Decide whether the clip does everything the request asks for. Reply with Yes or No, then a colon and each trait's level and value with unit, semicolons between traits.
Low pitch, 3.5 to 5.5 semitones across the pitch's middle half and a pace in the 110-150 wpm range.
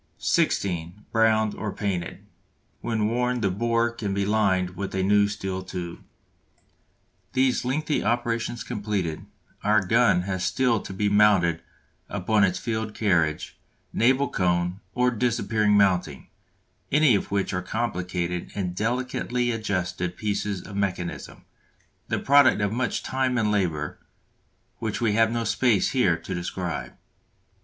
Yes: low, 105 Hz; average, 4.1 semitones; slow, 135 wpm